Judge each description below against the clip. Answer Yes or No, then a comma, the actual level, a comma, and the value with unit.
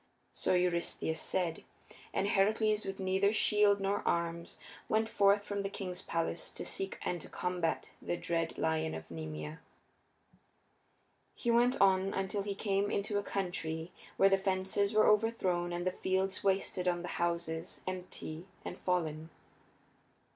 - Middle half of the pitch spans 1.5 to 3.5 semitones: Yes, average, 2.9 semitones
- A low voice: No, medium, 185 Hz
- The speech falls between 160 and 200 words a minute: No, average, 145 wpm